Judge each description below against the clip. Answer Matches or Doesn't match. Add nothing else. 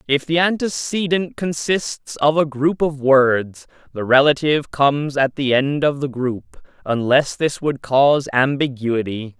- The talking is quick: Doesn't match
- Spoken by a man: Matches